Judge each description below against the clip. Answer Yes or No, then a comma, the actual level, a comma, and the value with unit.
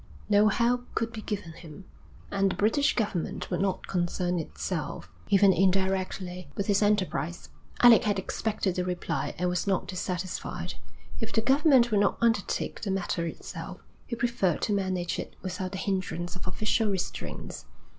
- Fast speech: No, average, 160 wpm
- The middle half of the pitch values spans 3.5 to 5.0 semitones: No, average, 2.9 semitones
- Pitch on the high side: Yes, high, 195 Hz